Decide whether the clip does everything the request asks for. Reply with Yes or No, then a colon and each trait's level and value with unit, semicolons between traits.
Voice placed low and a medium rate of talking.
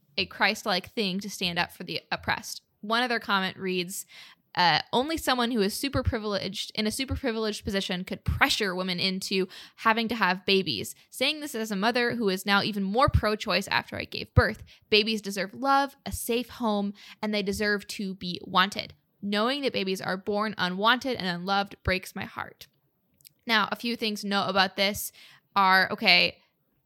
No: high, 205 Hz; average, 180 wpm